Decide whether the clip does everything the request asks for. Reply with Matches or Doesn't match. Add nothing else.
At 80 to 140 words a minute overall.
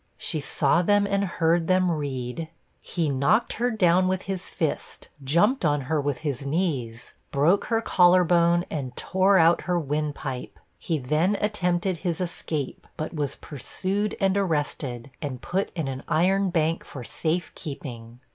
Doesn't match